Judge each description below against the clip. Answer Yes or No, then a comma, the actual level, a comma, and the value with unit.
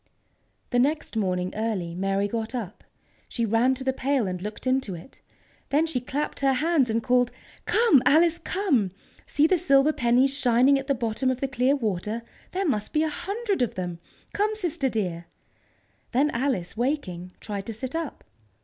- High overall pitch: Yes, very high, 255 Hz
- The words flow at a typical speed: Yes, average, 175 wpm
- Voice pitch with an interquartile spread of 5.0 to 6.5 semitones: Yes, average, 5.3 semitones